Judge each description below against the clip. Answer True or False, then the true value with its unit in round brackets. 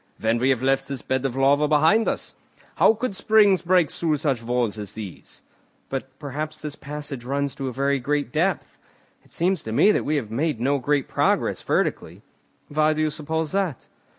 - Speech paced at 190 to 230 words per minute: True (195 wpm)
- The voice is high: False (145 Hz)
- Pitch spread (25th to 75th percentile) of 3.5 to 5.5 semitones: False (3.0 semitones)